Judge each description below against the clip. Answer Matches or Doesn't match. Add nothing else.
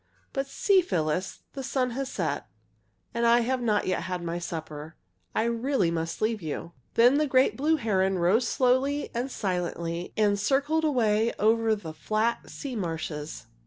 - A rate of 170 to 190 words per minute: Doesn't match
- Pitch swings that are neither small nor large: Doesn't match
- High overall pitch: Matches